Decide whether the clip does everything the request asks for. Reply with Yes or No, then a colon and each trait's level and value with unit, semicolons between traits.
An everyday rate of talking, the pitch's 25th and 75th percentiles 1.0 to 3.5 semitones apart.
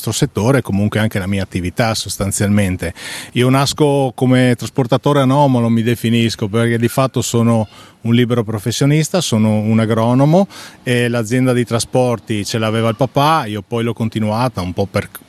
Yes: average, 155 wpm; average, 2.9 semitones